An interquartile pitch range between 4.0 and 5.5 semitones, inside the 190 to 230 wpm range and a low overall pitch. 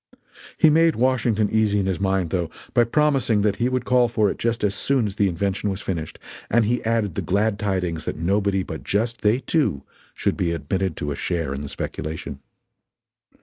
Yes: average, 4.3 semitones; average, 200 wpm; low, 100 Hz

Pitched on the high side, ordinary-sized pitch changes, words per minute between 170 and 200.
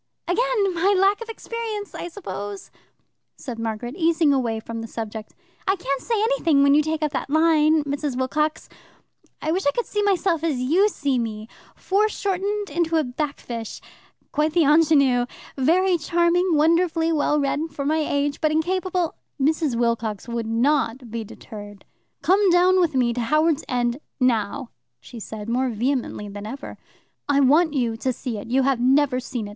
No: very high, 290 Hz; wide, 5.8 semitones; average, 175 wpm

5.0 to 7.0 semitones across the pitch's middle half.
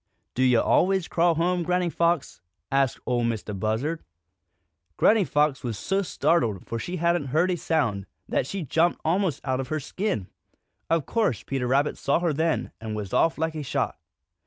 Yes: wide, 5.6 semitones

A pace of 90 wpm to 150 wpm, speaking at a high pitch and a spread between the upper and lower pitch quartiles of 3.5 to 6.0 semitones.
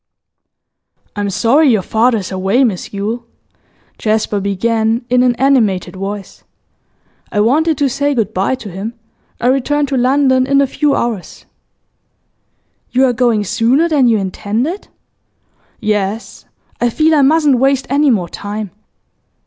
Yes: average, 140 wpm; high, 235 Hz; average, 4.8 semitones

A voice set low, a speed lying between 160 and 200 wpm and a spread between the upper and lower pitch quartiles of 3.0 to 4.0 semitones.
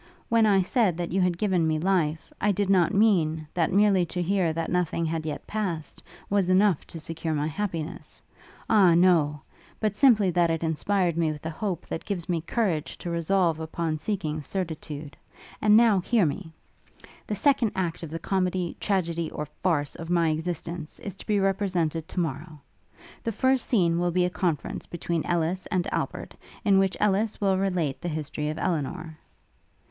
No: medium, 175 Hz; average, 180 wpm; average, 3.4 semitones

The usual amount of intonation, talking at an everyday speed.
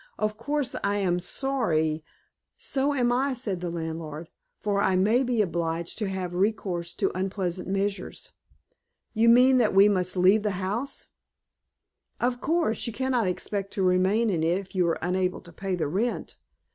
Yes: average, 4.5 semitones; average, 170 wpm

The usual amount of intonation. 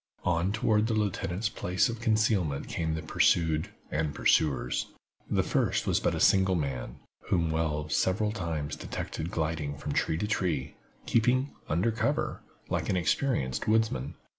No: wide, 5.7 semitones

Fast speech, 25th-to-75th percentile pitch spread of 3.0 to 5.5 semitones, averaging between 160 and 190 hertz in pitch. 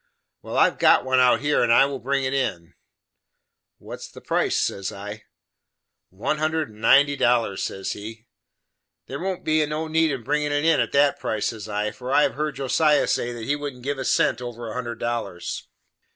No: fast, 210 wpm; average, 4.5 semitones; low, 130 Hz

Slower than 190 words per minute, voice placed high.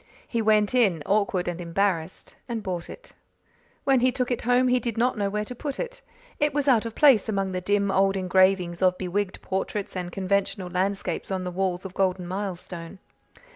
No: average, 195 wpm; high, 195 Hz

